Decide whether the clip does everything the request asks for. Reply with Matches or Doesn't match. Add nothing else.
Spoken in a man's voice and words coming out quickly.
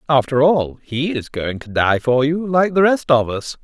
Matches